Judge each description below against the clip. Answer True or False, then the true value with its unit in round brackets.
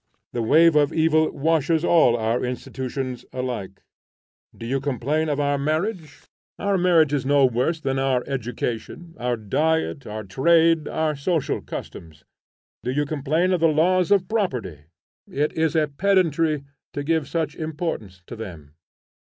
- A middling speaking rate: True (150 wpm)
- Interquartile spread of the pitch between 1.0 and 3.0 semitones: False (4.4 semitones)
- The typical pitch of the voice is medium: True (145 Hz)